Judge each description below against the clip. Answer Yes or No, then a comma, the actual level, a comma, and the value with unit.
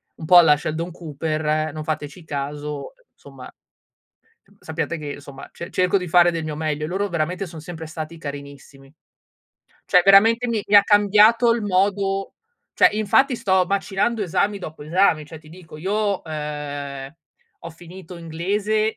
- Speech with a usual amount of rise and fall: Yes, average, 4.4 semitones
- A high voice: No, medium, 170 Hz